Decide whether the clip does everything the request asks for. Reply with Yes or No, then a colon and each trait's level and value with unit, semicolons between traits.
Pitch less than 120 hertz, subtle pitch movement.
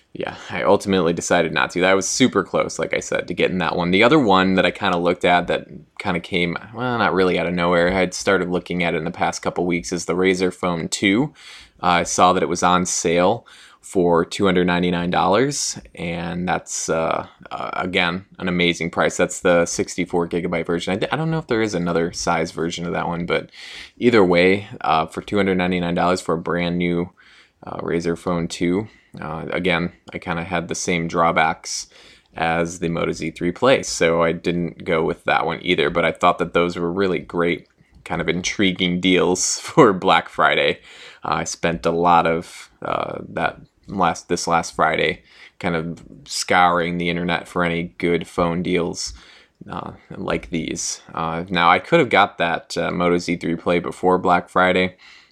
Yes: very low, 85 Hz; narrow, 1.3 semitones